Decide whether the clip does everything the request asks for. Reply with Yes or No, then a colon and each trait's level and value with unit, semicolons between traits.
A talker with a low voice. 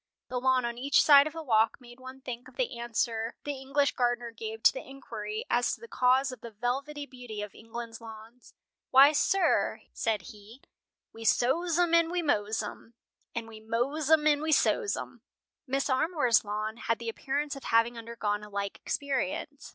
No: high, 245 Hz